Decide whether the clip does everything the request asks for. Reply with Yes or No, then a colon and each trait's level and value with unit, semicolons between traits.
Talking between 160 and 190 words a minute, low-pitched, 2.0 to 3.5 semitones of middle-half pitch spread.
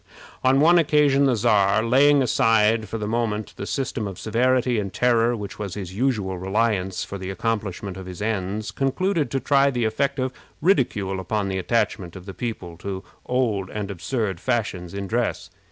No: average, 180 wpm; low, 110 Hz; average, 4.7 semitones